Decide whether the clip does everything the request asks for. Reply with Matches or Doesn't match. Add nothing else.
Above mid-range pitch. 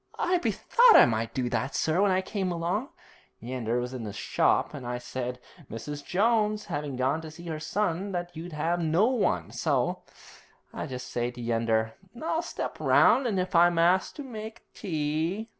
Doesn't match